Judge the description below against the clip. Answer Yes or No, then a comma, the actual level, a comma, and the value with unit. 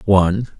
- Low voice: Yes, low, 100 Hz